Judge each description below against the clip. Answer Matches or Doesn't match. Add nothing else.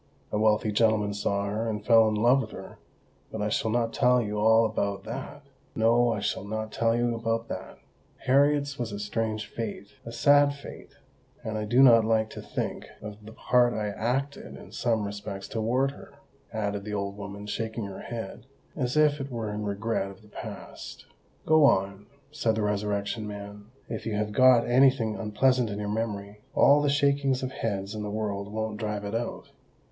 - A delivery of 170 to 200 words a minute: Matches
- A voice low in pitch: Matches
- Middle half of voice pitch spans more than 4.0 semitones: Doesn't match